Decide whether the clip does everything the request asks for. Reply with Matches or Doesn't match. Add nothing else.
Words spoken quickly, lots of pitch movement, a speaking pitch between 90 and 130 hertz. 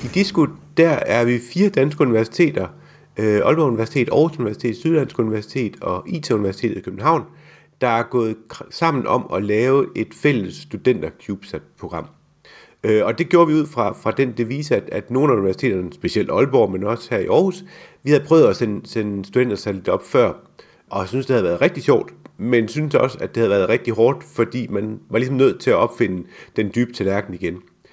Doesn't match